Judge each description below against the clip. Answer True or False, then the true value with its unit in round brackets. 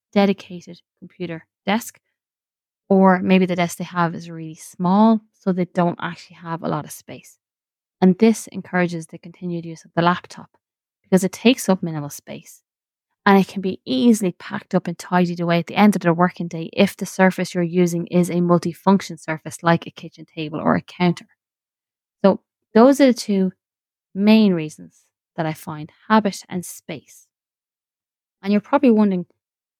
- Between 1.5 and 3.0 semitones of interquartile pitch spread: True (2.6 semitones)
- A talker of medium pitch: True (180 Hz)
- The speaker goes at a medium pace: True (175 wpm)